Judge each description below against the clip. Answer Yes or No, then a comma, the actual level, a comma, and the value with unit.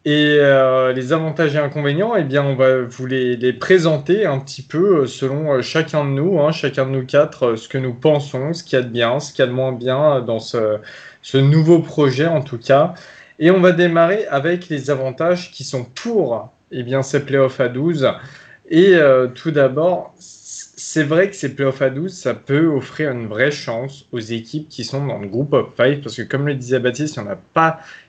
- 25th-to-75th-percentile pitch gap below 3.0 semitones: No, average, 3.5 semitones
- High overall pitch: No, medium, 140 Hz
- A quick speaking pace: Yes, fast, 225 wpm